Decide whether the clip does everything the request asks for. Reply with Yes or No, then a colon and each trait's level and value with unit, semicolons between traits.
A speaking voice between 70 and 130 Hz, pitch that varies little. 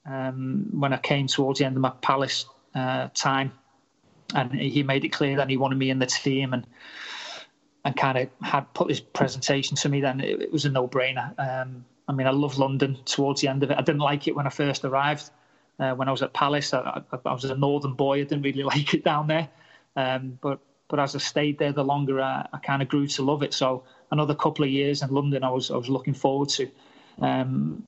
No: medium, 140 Hz; narrow, 1.4 semitones